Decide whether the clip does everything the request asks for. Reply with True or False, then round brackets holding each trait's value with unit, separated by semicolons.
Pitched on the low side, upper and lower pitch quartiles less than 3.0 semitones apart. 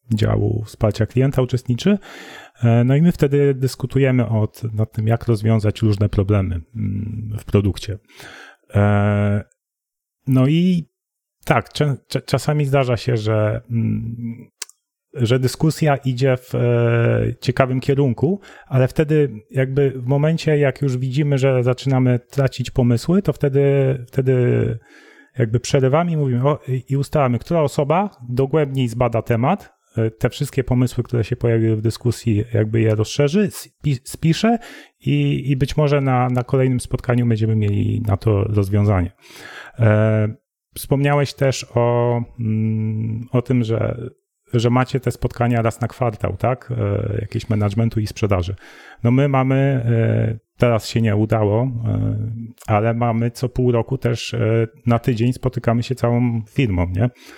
False (120 Hz; 3.3 semitones)